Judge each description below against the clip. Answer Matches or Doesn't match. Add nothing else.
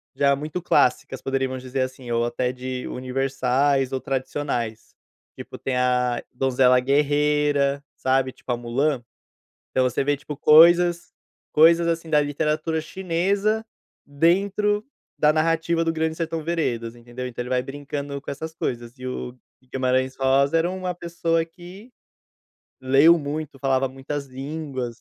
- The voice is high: Doesn't match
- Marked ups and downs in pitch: Doesn't match